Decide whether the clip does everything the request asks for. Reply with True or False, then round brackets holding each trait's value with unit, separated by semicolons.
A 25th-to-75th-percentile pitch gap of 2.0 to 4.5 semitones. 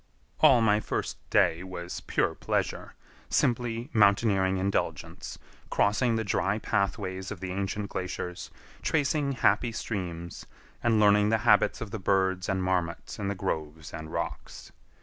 True (3.2 semitones)